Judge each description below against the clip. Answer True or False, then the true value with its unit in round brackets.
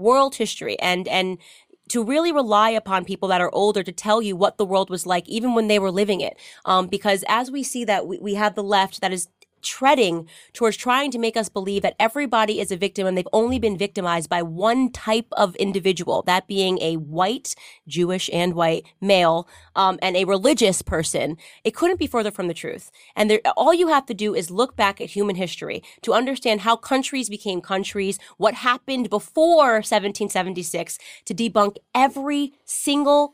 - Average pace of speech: True (195 wpm)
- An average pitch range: True (4.1 semitones)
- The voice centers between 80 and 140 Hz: False (205 Hz)